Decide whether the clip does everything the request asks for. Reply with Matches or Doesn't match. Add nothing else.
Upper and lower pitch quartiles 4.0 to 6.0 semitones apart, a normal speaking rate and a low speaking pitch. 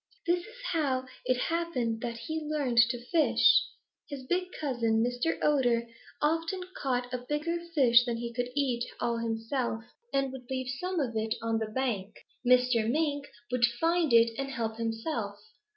Doesn't match